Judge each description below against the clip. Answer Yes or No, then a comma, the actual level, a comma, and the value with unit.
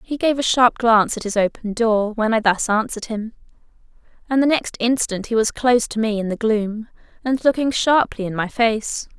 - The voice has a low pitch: No, high, 225 Hz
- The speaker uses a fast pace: Yes, fast, 210 wpm